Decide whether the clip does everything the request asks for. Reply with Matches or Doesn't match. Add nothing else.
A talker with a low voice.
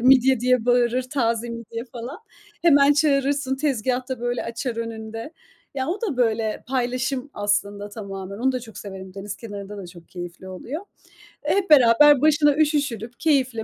Doesn't match